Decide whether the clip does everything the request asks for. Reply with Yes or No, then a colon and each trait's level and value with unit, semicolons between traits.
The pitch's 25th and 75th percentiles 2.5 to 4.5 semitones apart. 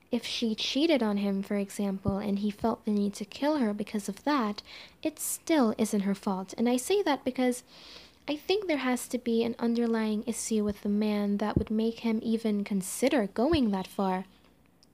Yes: average, 3.4 semitones